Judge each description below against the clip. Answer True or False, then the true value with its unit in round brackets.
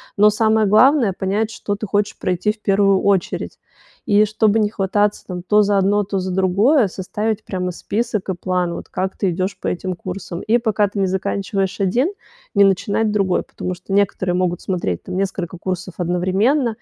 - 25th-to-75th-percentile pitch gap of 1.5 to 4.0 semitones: True (2.4 semitones)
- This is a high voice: True (195 Hz)